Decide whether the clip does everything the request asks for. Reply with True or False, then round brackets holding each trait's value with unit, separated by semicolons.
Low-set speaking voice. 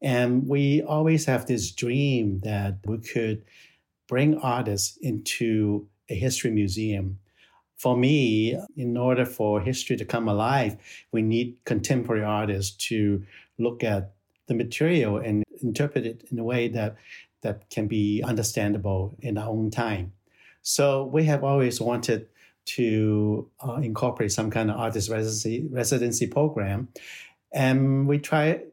True (115 Hz)